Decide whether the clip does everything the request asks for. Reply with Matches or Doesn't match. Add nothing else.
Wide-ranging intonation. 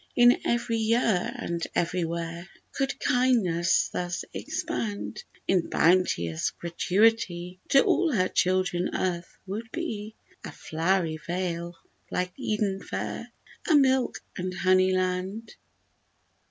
Doesn't match